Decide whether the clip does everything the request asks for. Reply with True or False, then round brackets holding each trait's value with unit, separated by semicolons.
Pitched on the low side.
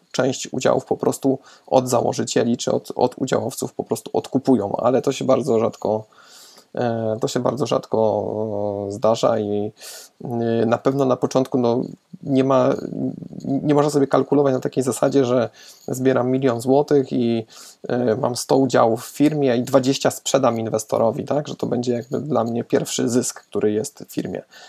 True (125 Hz)